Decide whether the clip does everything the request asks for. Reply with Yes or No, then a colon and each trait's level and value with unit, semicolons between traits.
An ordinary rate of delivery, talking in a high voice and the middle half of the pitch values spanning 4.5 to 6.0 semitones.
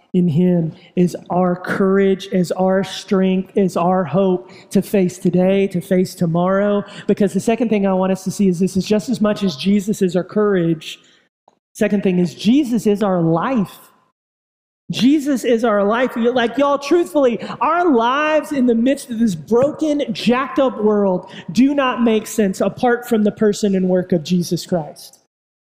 No: average, 175 wpm; high, 200 Hz; average, 4.1 semitones